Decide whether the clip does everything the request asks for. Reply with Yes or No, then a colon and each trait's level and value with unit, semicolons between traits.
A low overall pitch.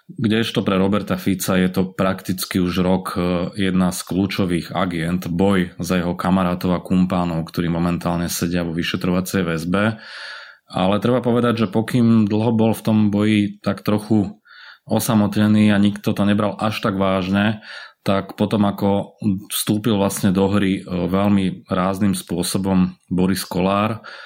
Yes: very low, 95 Hz